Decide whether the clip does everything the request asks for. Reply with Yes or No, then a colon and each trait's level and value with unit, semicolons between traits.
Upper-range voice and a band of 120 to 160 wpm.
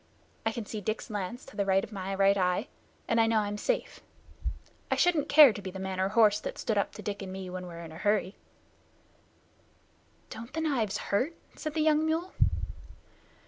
No: high, 210 Hz; fast, 205 wpm